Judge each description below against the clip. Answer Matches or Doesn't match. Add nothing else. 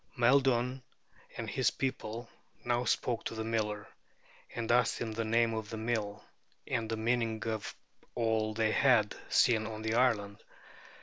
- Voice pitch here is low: Matches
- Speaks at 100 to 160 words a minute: Matches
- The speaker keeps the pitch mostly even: Matches